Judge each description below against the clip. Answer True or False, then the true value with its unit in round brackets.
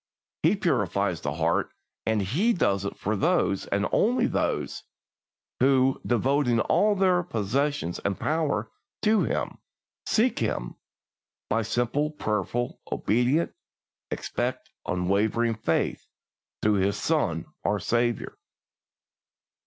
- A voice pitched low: True (120 Hz)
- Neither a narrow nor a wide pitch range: False (6.8 semitones)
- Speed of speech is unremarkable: False (110 wpm)